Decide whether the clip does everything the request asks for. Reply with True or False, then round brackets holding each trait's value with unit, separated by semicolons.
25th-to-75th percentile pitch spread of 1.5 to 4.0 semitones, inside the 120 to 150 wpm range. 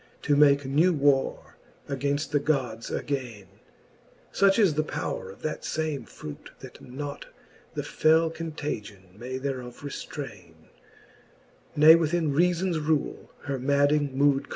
True (2.8 semitones; 135 wpm)